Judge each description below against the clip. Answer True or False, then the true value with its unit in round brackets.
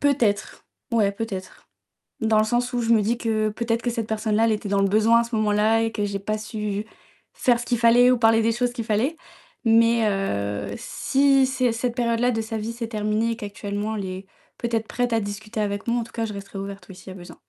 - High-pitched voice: True (225 Hz)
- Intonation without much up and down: True (2.1 semitones)